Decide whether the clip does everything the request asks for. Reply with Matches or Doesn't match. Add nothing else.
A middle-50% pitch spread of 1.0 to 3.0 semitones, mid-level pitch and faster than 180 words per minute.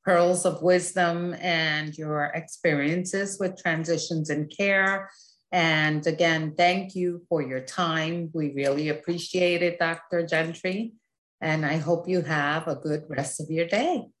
Doesn't match